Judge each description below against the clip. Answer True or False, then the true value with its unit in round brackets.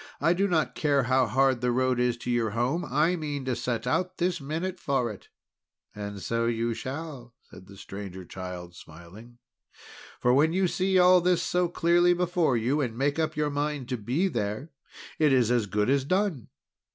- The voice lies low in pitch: True (130 Hz)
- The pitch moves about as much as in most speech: False (5.9 semitones)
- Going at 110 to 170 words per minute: False (190 wpm)